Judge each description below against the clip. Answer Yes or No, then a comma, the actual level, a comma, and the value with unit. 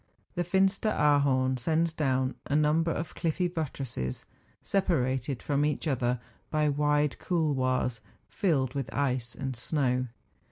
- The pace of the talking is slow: Yes, slow, 125 wpm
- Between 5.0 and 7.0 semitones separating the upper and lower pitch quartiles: No, average, 3.7 semitones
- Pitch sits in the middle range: Yes, medium, 145 Hz